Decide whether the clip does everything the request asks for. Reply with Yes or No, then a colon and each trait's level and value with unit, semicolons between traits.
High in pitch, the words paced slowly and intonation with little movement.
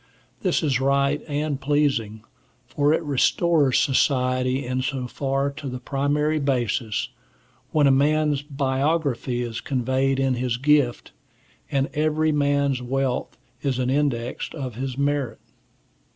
No: low, 135 Hz; slow, 130 wpm; narrow, 2.3 semitones